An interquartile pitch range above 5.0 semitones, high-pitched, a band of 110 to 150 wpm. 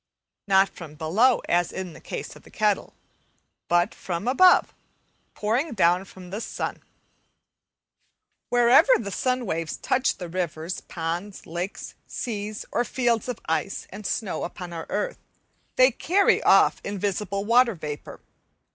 Yes: wide, 5.5 semitones; high, 200 Hz; average, 140 wpm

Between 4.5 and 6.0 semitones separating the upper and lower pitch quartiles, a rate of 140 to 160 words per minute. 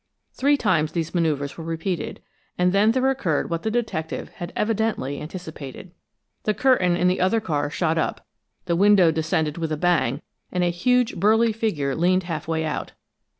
No: average, 4.8 semitones; average, 175 wpm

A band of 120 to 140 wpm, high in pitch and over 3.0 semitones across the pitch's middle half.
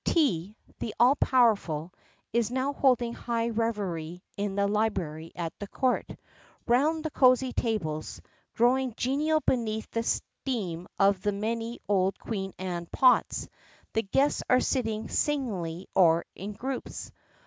Yes: slow, 135 wpm; high, 220 Hz; average, 5.1 semitones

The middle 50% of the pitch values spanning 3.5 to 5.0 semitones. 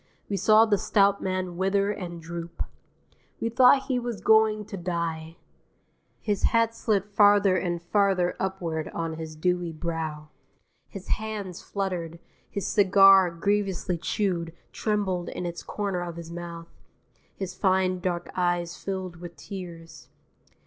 No: average, 2.9 semitones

